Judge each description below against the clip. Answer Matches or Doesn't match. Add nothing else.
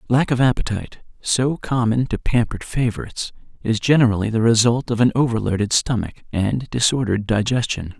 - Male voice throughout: Matches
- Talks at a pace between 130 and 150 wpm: Matches